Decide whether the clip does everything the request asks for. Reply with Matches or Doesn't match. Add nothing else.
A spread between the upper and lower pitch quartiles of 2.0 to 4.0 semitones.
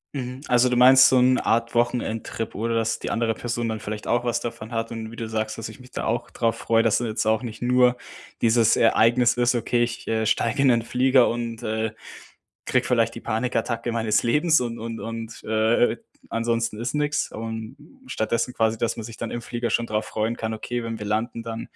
Doesn't match